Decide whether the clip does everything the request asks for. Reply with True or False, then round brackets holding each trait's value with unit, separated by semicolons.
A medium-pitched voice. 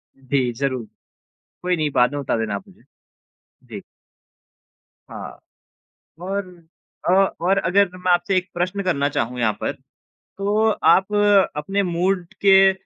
True (180 Hz)